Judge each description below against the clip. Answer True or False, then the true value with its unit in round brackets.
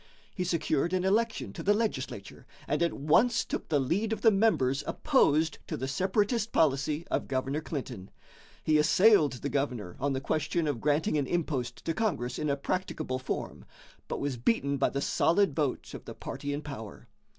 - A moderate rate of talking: True (185 wpm)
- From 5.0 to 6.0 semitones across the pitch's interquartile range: True (5.3 semitones)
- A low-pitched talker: False (150 Hz)